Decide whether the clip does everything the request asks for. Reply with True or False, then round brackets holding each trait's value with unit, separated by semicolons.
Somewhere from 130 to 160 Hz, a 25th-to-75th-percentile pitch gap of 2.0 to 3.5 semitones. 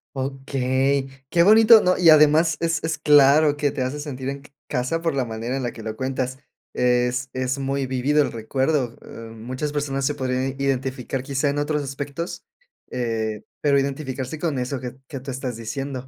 True (135 Hz; 2.4 semitones)